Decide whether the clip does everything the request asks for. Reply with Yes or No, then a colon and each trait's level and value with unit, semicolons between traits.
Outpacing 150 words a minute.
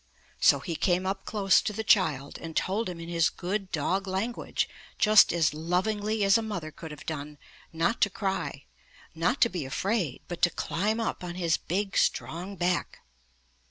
Yes: average, 180 wpm